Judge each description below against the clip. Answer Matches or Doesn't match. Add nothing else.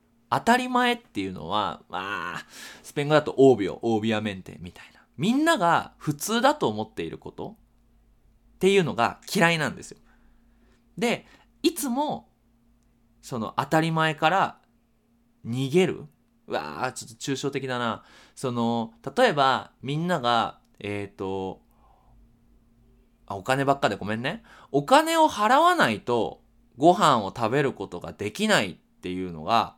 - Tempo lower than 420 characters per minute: Matches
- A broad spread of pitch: Matches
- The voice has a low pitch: Matches